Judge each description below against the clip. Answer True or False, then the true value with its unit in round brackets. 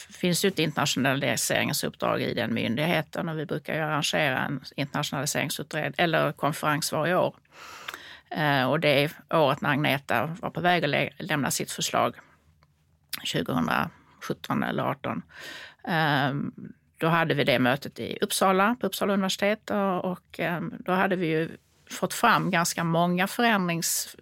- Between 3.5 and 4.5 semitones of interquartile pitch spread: True (3.9 semitones)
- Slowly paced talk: False (140 wpm)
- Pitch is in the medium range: True (180 Hz)